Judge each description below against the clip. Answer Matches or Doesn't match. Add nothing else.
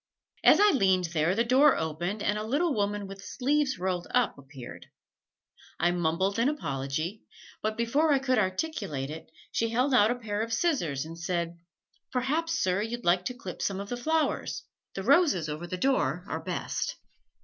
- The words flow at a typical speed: Matches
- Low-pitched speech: Doesn't match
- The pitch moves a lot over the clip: Matches